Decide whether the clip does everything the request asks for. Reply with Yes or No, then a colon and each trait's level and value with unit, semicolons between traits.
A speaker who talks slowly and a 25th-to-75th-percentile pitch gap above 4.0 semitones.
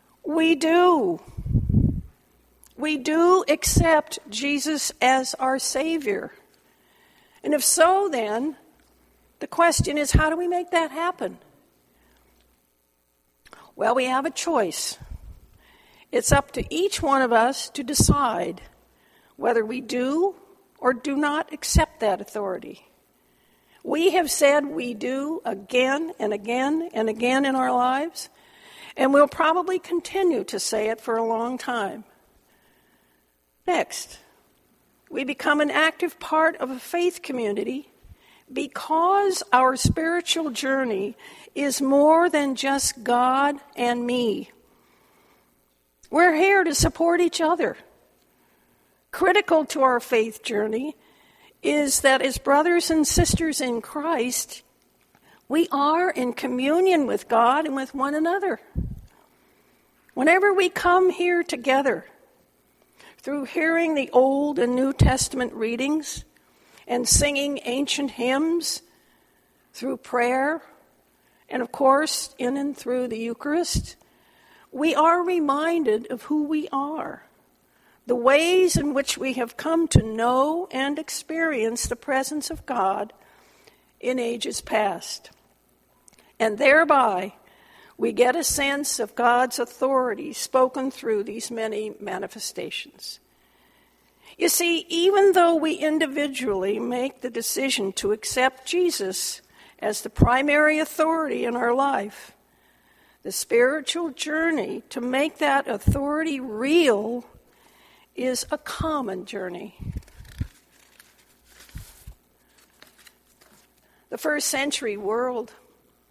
Yes: slow, 115 wpm; average, 5.0 semitones